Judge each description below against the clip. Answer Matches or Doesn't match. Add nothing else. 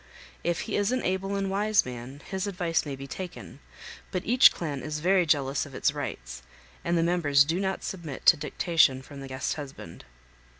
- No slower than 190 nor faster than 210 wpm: Matches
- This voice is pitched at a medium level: Matches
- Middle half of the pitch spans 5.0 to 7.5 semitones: Matches